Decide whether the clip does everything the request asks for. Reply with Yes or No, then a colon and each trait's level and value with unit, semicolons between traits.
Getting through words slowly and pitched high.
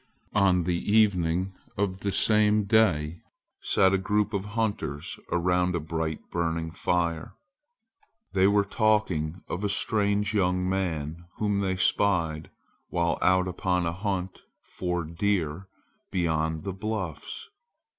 No: slow, 125 wpm; very low, 90 Hz